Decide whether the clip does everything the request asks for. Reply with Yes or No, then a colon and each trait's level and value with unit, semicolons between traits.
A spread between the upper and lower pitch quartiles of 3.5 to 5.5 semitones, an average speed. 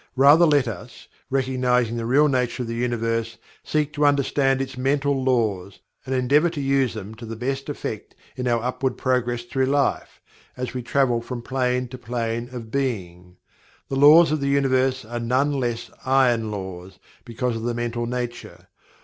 No: narrow, 2.6 semitones; average, 175 wpm